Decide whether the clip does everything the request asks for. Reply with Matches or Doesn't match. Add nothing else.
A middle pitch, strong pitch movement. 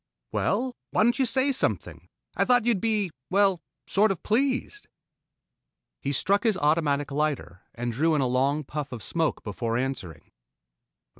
Matches